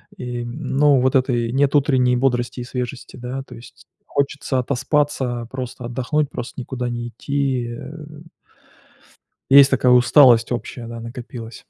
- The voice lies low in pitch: Yes, low, 125 Hz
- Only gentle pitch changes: Yes, narrow, 2.2 semitones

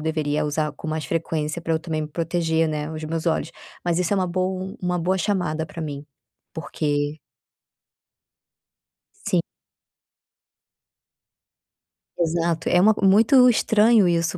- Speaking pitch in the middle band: Yes, medium, 165 Hz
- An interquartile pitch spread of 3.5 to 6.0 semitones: No, narrow, 2.6 semitones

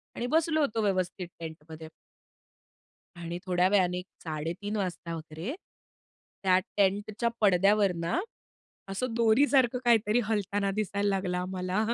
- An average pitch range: Yes, average, 3.4 semitones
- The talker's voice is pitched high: Yes, high, 195 Hz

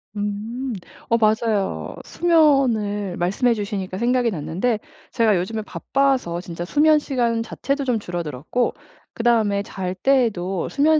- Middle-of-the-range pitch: No, high, 220 Hz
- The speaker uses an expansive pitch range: No, average, 4.8 semitones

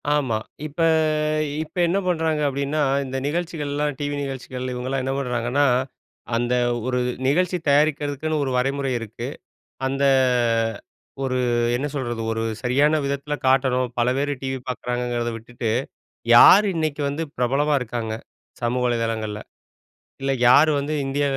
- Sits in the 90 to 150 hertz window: Yes, low, 135 Hz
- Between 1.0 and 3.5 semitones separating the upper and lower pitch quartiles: Yes, average, 3.0 semitones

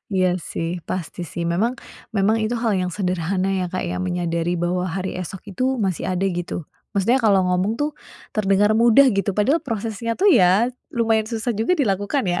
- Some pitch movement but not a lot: Yes, average, 3.8 semitones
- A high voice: Yes, high, 195 Hz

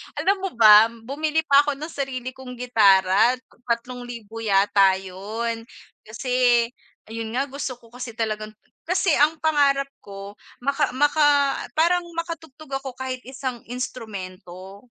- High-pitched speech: Yes, very high, 250 Hz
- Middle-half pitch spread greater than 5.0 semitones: No, average, 4.2 semitones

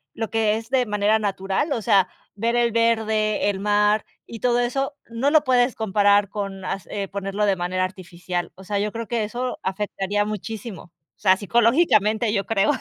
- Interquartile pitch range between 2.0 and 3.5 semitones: Yes, average, 2.7 semitones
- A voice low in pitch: No, high, 210 Hz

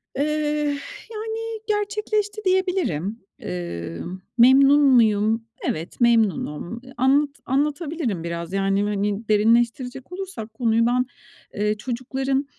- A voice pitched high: Yes, high, 245 Hz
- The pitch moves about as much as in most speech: No, wide, 6.4 semitones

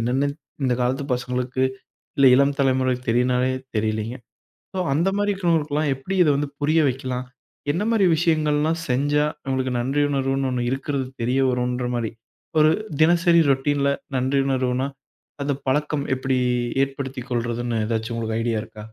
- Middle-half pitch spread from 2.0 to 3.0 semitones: Yes, average, 2.7 semitones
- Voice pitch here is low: Yes, low, 130 Hz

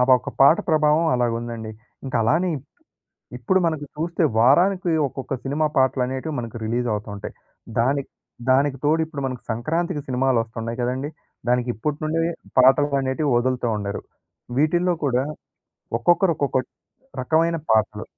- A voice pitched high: No, low, 135 Hz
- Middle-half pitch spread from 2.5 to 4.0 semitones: No, average, 4.4 semitones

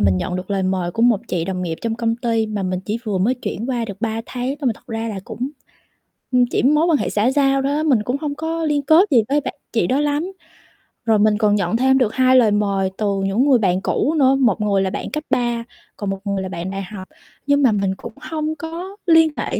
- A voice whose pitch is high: Yes, high, 230 Hz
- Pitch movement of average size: No, wide, 5.7 semitones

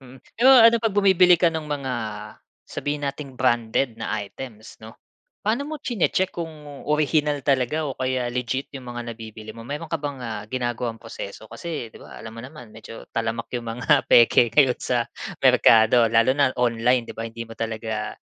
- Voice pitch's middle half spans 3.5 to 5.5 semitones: Yes, average, 4.6 semitones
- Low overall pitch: Yes, low, 125 Hz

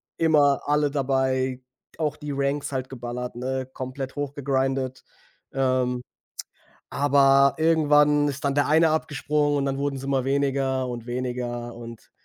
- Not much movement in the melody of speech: Yes, narrow, 1.9 semitones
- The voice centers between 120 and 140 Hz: Yes, low, 135 Hz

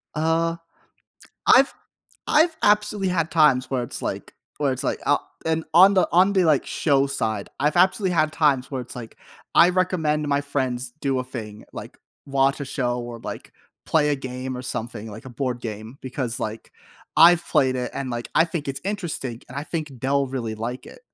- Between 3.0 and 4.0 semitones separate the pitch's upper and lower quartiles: No, average, 4.6 semitones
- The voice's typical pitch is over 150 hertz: No, medium, 140 Hz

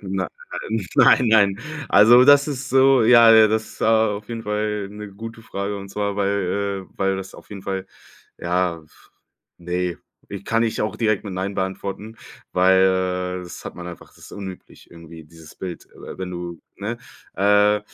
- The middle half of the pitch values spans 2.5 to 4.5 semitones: Yes, average, 2.9 semitones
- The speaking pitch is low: Yes, low, 100 Hz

